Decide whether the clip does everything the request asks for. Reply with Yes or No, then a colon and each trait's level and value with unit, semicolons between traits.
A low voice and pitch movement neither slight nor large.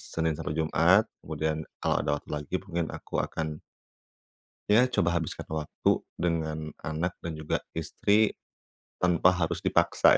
No: very low, 80 Hz; narrow, 2.1 semitones